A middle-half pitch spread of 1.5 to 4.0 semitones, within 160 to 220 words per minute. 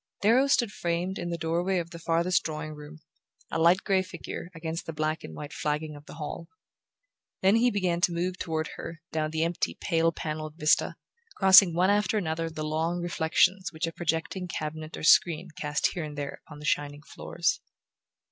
Yes: narrow, 2.6 semitones; average, 195 wpm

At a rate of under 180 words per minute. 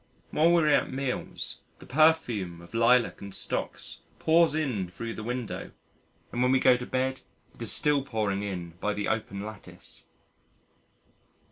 Yes: average, 160 wpm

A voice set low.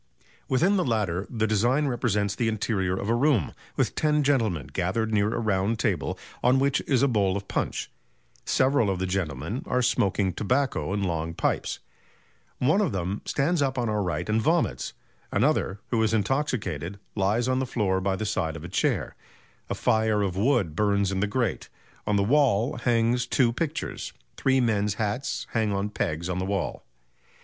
Yes: low, 110 Hz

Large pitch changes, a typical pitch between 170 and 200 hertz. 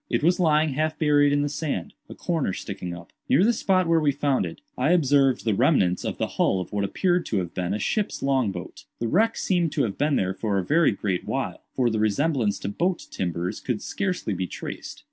No: wide, 8.2 semitones; low, 135 Hz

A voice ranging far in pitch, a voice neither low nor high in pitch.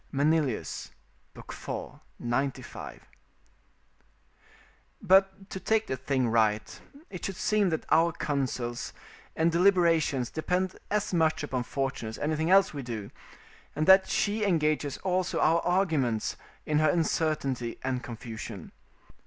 Yes: wide, 5.8 semitones; medium, 155 Hz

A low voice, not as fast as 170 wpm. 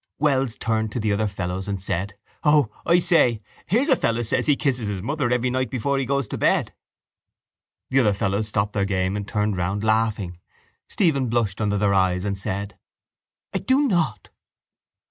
No: low, 110 Hz; average, 185 wpm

